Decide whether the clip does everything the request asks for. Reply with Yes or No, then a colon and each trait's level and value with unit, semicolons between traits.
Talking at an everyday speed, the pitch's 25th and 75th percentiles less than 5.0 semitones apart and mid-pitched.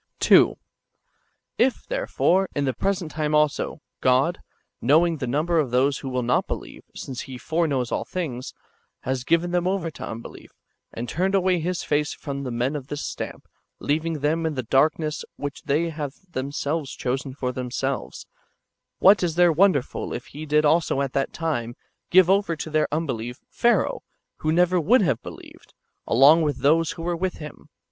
Yes: average, 175 wpm; average, 4.1 semitones; medium, 150 Hz